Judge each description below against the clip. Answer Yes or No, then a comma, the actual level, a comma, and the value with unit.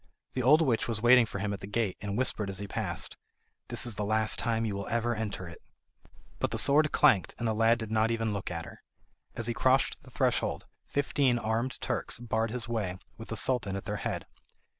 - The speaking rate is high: Yes, fast, 225 wpm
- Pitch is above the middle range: No, low, 115 Hz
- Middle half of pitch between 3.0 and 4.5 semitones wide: No, narrow, 2.6 semitones